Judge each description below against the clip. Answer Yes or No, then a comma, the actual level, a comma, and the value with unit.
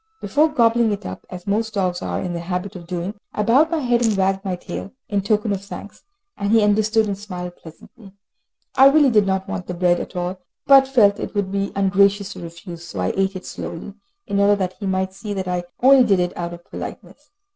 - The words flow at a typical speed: No, fast, 230 wpm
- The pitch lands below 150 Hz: No, high, 200 Hz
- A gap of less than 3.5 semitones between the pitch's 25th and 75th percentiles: Yes, average, 3.0 semitones